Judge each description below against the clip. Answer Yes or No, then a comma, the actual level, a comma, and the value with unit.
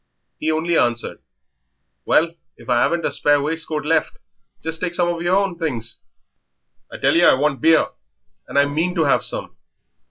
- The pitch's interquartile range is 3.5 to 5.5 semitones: No, average, 3.0 semitones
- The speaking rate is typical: Yes, average, 180 wpm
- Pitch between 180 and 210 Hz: No, medium, 160 Hz